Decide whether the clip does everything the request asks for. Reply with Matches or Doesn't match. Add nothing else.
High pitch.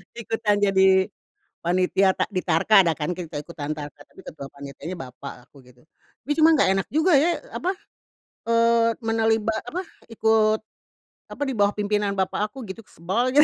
Matches